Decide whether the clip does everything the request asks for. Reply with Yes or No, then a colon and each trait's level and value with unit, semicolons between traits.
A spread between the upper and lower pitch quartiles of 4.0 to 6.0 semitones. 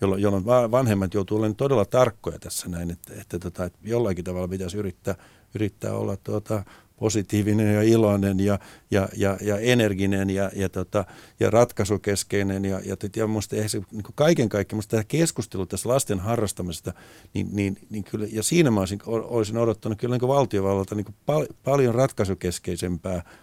No: narrow, 2.6 semitones